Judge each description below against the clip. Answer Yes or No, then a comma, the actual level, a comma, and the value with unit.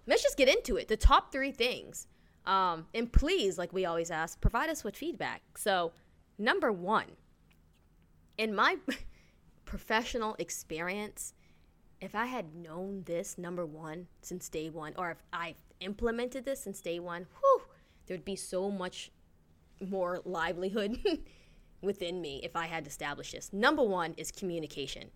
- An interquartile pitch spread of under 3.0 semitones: No, average, 5.3 semitones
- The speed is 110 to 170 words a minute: Yes, average, 150 wpm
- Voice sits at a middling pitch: Yes, medium, 180 Hz